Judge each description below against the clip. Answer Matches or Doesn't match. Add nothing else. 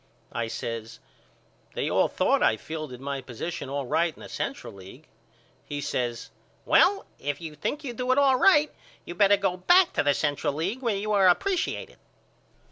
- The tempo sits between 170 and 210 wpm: Matches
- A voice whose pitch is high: Doesn't match